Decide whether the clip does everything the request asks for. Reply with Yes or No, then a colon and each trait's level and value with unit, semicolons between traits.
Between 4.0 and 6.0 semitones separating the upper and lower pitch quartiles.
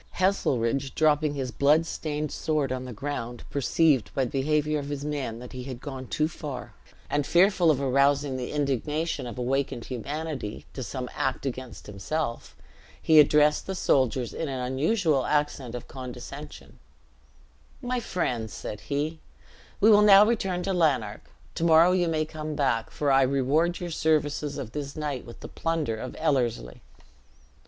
No: average, 3.6 semitones